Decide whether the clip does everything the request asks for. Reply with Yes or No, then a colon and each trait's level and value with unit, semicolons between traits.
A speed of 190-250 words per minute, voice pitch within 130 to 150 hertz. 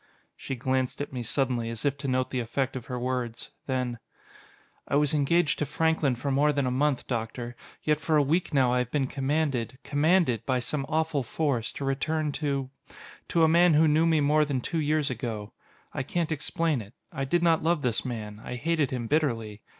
Yes: fast, 205 wpm; low, 135 Hz